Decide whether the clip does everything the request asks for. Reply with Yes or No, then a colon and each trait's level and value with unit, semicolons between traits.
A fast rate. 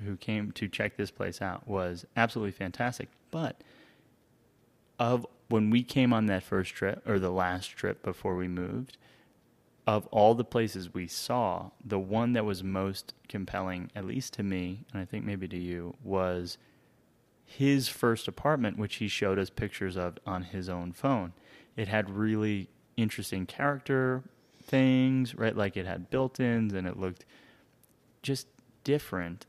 No: average, 160 wpm